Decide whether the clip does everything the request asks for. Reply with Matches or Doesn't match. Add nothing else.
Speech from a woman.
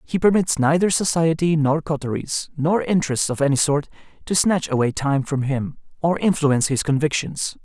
Doesn't match